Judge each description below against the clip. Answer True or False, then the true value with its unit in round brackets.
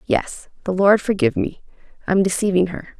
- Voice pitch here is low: False (195 Hz)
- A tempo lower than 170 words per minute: True (140 wpm)